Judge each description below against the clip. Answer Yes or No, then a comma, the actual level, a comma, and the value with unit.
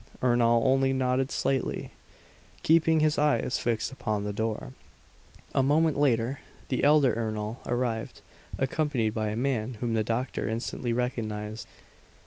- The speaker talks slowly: Yes, slow, 130 wpm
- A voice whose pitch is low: Yes, low, 120 Hz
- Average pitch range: Yes, average, 3.2 semitones